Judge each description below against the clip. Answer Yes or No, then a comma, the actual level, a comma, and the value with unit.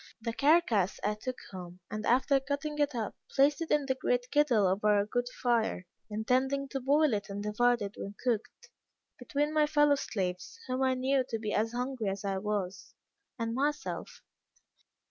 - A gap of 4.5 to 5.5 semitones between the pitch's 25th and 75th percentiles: Yes, average, 4.9 semitones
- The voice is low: No, high, 245 Hz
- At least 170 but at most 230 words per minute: Yes, average, 180 wpm